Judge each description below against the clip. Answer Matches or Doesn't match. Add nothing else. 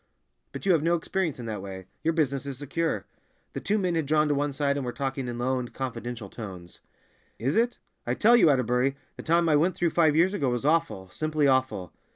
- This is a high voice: Doesn't match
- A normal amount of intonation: Matches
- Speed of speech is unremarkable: Doesn't match